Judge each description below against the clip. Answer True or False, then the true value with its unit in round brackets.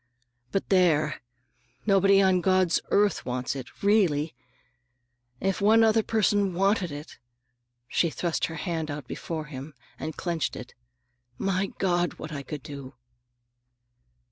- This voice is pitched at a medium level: True (165 Hz)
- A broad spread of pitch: True (6.3 semitones)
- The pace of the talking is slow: True (120 wpm)